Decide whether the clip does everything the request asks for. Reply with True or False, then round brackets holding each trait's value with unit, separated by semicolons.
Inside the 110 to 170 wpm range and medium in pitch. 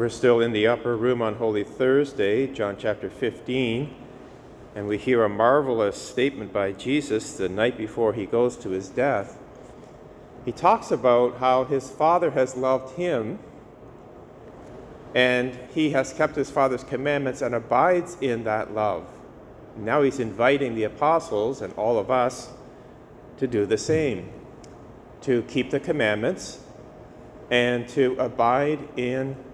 False (140 wpm; 125 Hz)